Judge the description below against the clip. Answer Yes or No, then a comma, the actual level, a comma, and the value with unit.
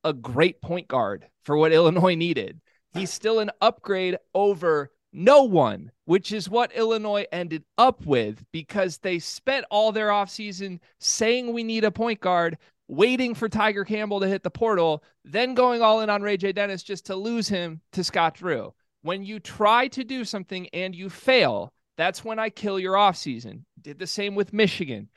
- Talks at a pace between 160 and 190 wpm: Yes, average, 185 wpm